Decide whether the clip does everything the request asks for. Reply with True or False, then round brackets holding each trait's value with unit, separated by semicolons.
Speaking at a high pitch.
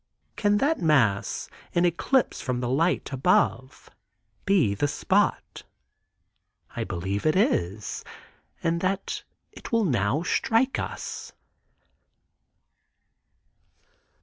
False (155 Hz)